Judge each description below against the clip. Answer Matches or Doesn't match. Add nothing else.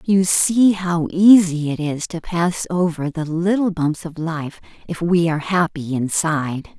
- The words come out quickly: Doesn't match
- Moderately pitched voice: Matches